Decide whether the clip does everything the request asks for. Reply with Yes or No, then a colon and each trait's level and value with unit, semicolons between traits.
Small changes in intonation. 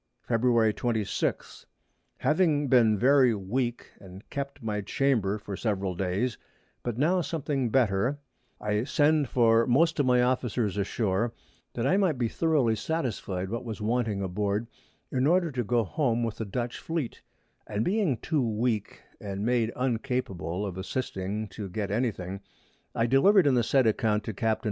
No: average, 4.1 semitones